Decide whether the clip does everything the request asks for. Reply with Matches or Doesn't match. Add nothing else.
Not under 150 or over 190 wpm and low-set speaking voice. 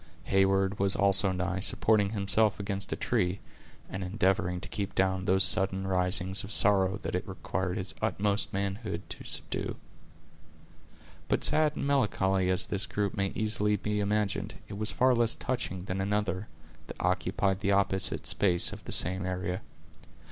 Matches